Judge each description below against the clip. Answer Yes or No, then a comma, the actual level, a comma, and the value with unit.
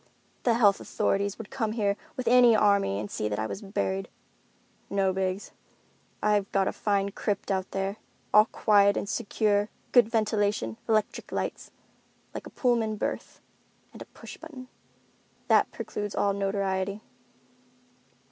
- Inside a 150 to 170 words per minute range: No, average, 140 wpm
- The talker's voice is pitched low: No, high, 205 Hz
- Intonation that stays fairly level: Yes, narrow, 2.0 semitones